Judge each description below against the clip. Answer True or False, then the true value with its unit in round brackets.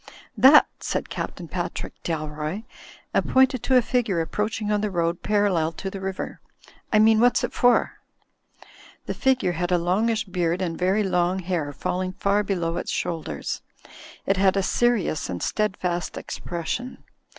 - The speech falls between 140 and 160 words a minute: True (155 wpm)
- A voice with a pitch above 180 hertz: True (190 Hz)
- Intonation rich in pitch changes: False (3.7 semitones)